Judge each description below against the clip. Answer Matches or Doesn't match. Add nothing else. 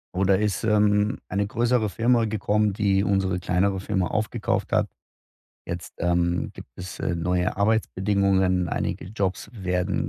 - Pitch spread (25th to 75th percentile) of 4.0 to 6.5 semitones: Doesn't match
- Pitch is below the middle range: Matches